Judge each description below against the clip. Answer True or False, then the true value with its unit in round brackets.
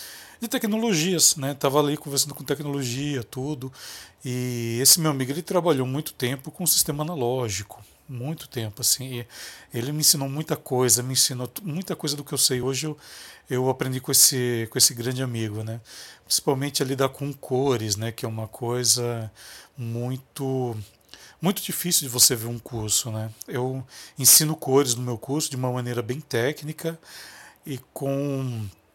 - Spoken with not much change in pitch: False (3.4 semitones)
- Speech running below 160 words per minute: False (165 wpm)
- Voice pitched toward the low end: True (130 Hz)